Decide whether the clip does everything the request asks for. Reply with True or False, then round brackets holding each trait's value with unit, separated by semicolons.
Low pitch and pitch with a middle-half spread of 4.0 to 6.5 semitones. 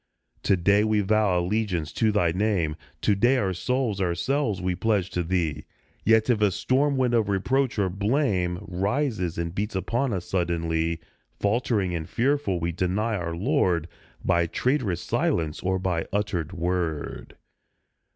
True (95 Hz; 4.3 semitones)